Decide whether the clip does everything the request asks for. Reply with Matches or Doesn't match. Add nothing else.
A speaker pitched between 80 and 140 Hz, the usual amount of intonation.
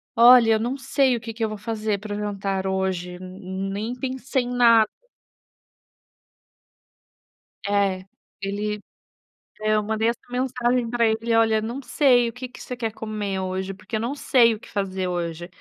Doesn't match